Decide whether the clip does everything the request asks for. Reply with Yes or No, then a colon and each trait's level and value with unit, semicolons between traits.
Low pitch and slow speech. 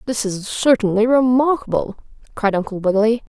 No: high, 225 Hz; slow, 125 wpm